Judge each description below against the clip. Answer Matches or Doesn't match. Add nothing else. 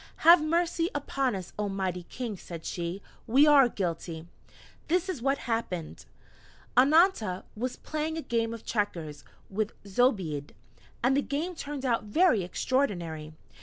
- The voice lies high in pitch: Matches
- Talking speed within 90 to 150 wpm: Matches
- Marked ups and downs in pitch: Matches